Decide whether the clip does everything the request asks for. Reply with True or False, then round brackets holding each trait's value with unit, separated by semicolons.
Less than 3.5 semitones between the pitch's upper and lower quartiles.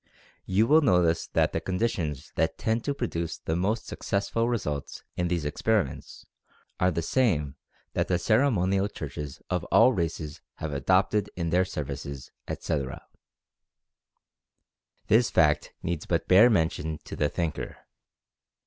False (5.4 semitones)